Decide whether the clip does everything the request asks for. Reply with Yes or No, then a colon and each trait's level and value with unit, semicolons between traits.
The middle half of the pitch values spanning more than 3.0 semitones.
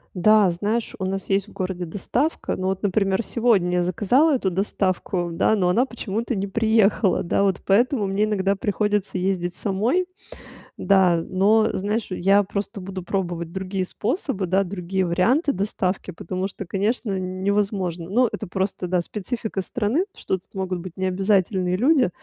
No: narrow, 2.5 semitones